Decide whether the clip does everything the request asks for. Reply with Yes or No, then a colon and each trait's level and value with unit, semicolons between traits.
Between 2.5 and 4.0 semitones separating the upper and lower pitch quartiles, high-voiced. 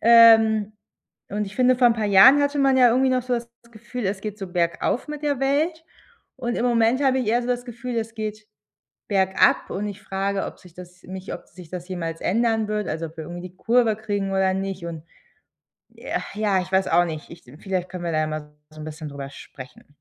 No: average, 4.8 semitones; high, 205 Hz